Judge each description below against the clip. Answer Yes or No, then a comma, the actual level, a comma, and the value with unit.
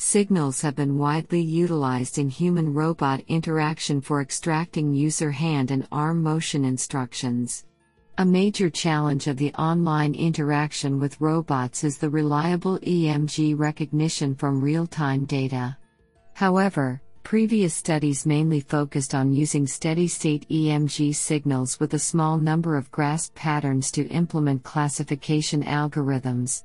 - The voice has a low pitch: No, medium, 150 Hz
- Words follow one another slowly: Yes, slow, 130 wpm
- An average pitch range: No, narrow, 2.1 semitones